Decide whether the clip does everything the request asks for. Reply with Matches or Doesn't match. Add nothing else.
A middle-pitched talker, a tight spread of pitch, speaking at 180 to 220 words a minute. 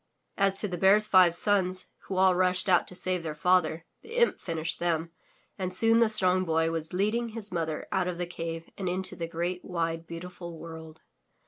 Matches